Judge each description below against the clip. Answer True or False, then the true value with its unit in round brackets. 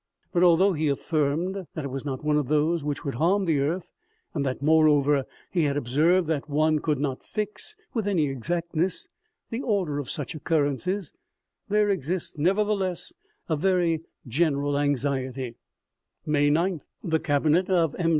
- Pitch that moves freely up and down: False (3.9 semitones)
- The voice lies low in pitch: False (155 Hz)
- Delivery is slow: False (160 wpm)